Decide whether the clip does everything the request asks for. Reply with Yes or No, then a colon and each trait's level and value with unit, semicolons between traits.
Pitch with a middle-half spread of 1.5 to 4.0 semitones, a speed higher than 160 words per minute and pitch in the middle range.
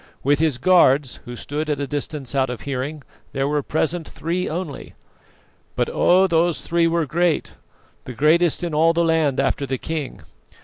Yes: average, 3.3 semitones; average, 175 wpm; medium, 150 Hz